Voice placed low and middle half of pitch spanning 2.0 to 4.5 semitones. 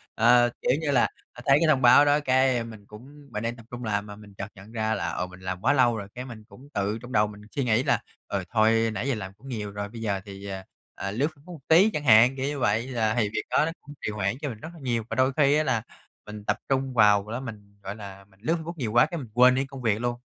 Yes: low, 115 Hz; average, 4.2 semitones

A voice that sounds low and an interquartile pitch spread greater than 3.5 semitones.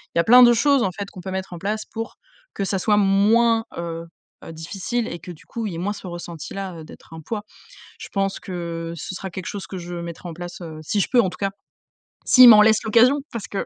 No: high, 195 Hz; average, 4.1 semitones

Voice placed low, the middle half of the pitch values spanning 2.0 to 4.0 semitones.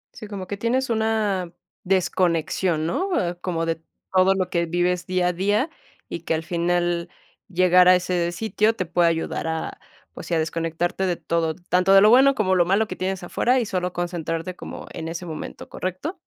No: medium, 180 Hz; narrow, 2.4 semitones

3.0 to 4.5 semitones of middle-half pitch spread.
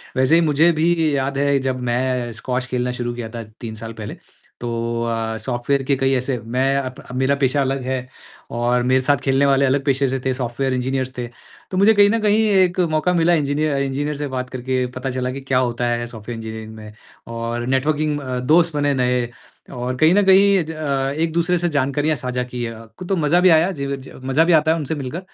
Yes: average, 3.6 semitones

